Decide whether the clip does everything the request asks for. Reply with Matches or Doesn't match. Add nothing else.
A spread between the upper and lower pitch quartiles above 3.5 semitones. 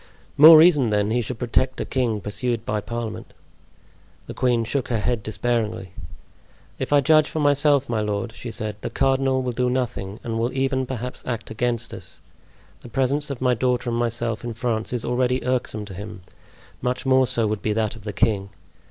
Doesn't match